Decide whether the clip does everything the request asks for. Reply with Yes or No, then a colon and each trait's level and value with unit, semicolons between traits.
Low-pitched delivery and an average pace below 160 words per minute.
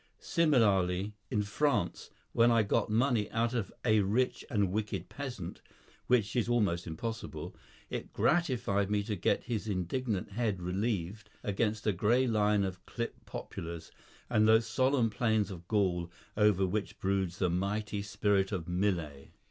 Yes: low, 105 Hz; average, 150 wpm